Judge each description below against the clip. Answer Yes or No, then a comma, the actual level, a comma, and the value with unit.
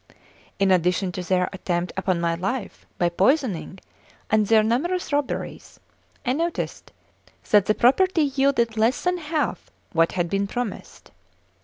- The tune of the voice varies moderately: No, wide, 7.1 semitones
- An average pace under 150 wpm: Yes, average, 140 wpm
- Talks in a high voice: Yes, high, 215 Hz